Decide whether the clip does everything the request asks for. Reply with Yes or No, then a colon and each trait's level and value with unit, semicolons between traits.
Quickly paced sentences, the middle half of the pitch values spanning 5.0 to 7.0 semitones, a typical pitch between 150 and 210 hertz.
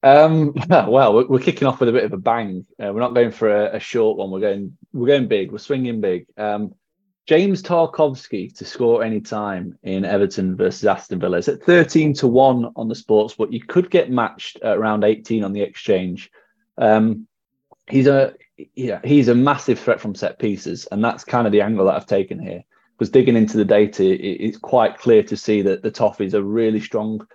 No: fast, 220 wpm; average, 5.3 semitones; low, 120 Hz